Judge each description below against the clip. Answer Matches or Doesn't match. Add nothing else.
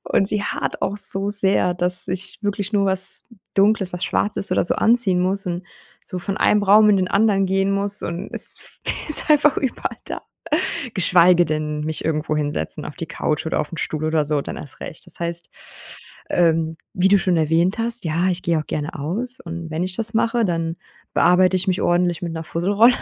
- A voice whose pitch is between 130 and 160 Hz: Doesn't match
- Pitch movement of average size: Matches